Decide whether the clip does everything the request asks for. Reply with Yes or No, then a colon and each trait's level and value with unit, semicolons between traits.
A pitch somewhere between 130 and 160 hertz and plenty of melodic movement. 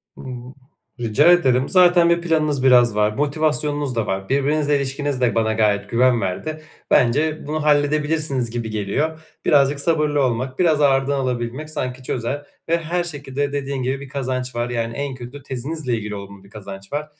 No: low, 135 Hz; average, 3.9 semitones